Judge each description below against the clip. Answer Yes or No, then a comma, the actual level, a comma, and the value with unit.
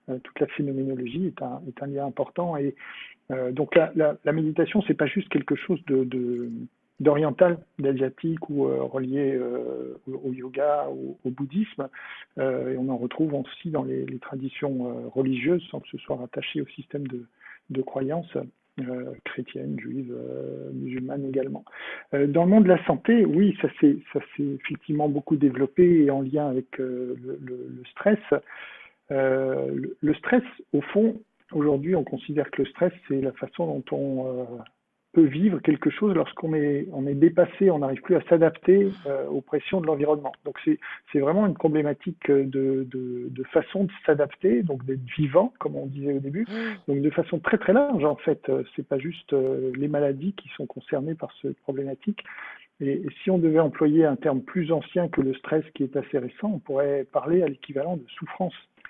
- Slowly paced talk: No, average, 190 wpm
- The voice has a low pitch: No, medium, 145 Hz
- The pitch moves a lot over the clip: No, average, 4.3 semitones